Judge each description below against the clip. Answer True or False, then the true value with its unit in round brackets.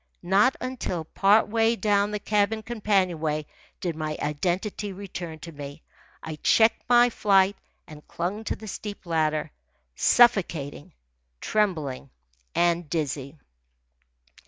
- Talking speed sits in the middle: False (115 wpm)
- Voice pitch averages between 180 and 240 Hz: True (185 Hz)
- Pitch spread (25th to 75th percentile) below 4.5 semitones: False (5.1 semitones)